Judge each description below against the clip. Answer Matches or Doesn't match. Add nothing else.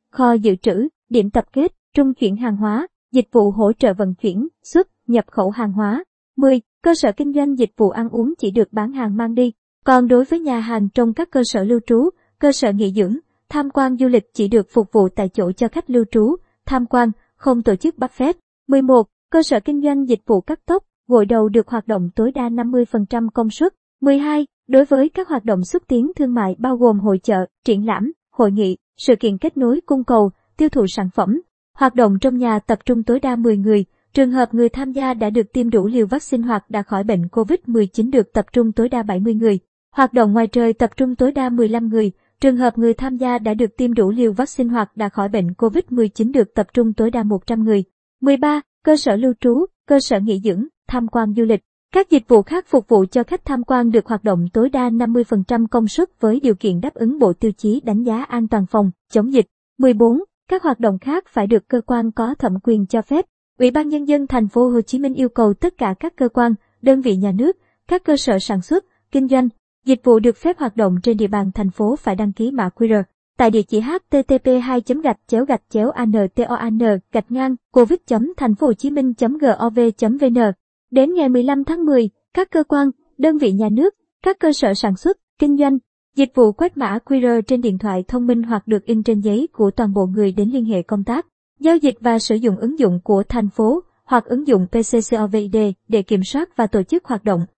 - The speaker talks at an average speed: Matches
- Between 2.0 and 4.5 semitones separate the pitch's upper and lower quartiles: Matches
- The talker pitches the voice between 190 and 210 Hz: Doesn't match